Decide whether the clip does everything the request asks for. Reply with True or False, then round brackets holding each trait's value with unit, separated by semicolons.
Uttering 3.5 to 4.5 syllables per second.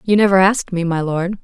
False (6.1 syllables/s)